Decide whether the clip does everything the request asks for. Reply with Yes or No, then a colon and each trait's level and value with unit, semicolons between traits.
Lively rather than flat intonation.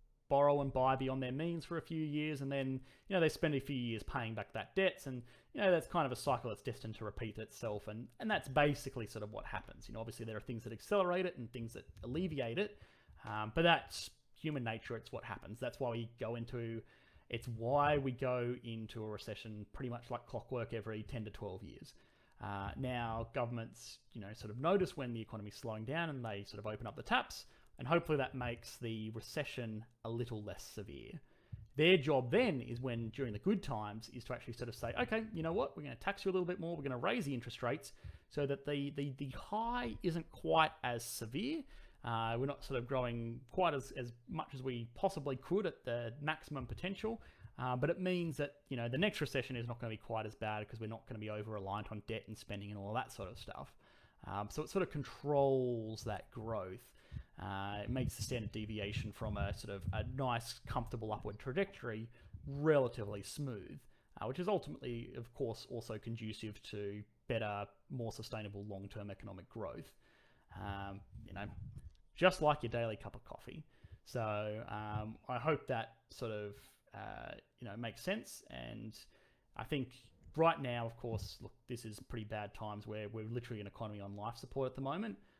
No: average, 4.3 semitones